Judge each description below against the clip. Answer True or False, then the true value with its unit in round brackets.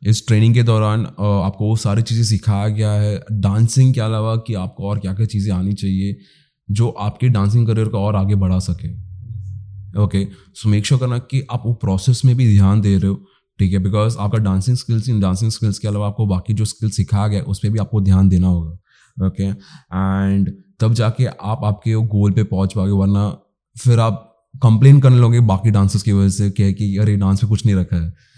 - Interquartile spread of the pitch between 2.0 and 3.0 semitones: True (2.4 semitones)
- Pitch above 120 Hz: False (105 Hz)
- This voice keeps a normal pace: False (215 wpm)